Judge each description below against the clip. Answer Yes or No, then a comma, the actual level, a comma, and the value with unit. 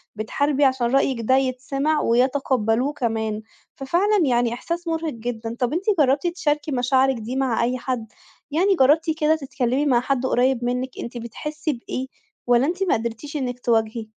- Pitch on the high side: Yes, very high, 260 Hz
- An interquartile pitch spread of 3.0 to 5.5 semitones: Yes, average, 3.6 semitones